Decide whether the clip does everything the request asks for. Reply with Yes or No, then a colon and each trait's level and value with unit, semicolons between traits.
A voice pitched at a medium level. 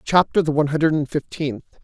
Yes: medium, 150 Hz